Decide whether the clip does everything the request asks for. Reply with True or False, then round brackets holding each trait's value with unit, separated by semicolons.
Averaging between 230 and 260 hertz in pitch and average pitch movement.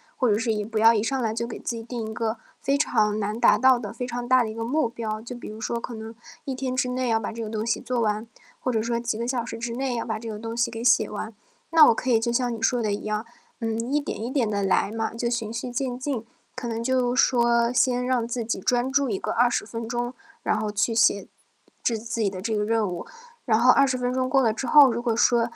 False (235 Hz; 2.0 semitones)